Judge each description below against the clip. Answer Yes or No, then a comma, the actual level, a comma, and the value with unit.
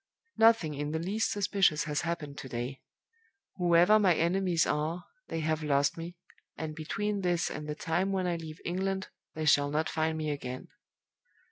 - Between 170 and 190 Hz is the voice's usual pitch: No, medium, 160 Hz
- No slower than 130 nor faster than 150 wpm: No, average, 170 wpm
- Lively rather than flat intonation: No, average, 3.4 semitones